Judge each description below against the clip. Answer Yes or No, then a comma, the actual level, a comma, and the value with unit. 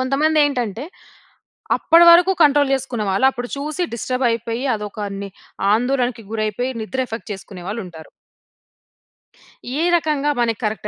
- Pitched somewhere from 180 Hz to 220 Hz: No, high, 245 Hz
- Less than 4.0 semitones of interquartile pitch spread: No, average, 4.6 semitones